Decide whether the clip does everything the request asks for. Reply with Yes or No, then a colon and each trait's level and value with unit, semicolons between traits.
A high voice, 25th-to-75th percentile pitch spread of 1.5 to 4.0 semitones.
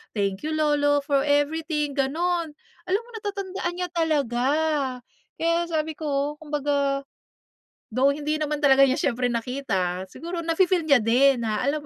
Yes: very high, 290 Hz; average, 2.9 semitones